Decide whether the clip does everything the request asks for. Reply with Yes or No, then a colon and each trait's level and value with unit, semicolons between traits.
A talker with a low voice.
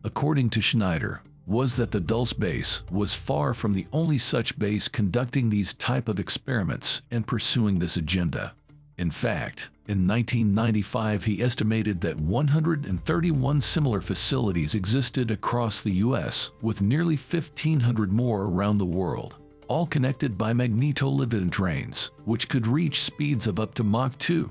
Yes: low, 115 Hz